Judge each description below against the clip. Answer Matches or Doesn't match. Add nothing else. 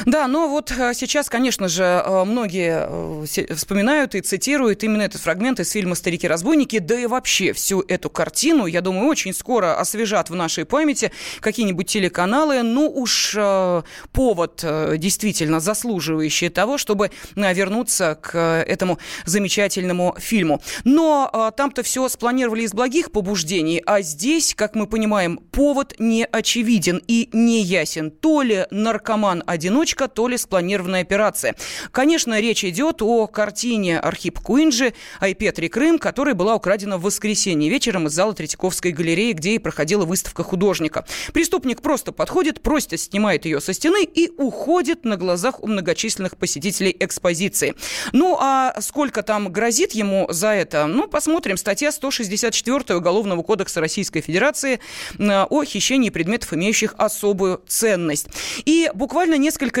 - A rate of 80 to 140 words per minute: Matches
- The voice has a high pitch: Matches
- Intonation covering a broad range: Matches